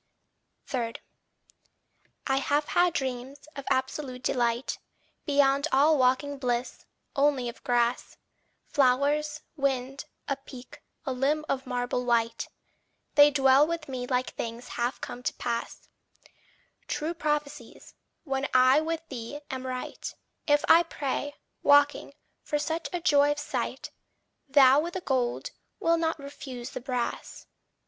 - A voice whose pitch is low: No, very high, 275 Hz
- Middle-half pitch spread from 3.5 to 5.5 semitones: No, average, 2.7 semitones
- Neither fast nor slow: No, slow, 130 wpm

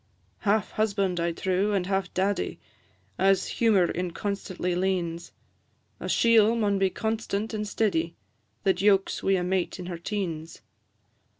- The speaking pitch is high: Yes, high, 195 Hz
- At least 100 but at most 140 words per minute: Yes, slow, 135 wpm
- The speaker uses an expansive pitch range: No, narrow, 2.5 semitones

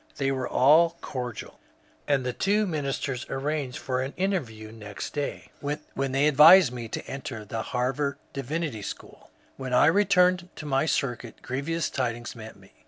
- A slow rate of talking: No, average, 160 wpm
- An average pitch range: Yes, average, 3.7 semitones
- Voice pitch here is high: No, low, 135 Hz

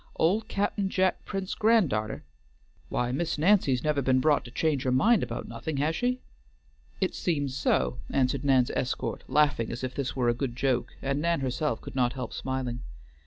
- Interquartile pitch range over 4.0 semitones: Yes, average, 4.7 semitones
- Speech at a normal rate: Yes, average, 185 wpm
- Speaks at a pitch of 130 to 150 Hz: Yes, low, 135 Hz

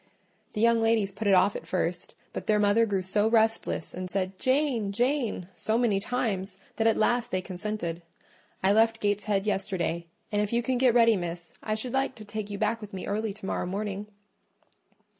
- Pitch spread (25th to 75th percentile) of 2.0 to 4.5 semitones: Yes, average, 2.8 semitones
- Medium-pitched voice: No, high, 210 Hz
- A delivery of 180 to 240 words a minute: Yes, average, 195 wpm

